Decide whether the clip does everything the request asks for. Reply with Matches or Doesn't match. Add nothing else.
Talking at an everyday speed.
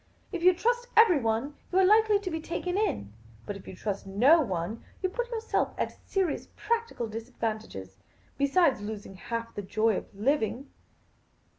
Matches